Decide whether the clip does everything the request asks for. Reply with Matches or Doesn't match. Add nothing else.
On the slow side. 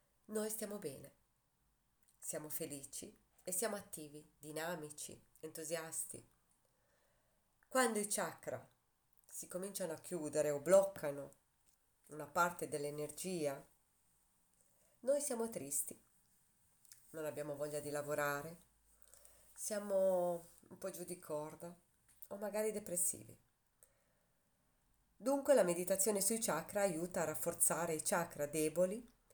Matches